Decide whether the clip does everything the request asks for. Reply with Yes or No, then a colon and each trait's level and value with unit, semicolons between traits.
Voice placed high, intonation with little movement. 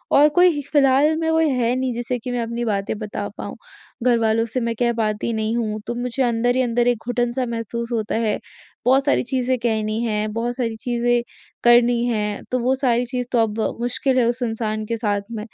Yes: high, 240 Hz; narrow, 2.0 semitones